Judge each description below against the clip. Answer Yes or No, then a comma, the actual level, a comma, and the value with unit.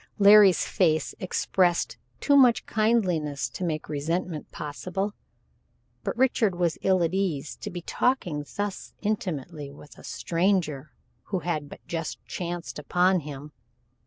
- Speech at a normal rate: No, slow, 130 wpm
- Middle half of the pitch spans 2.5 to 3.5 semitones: No, average, 4.3 semitones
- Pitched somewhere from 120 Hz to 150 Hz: No, medium, 175 Hz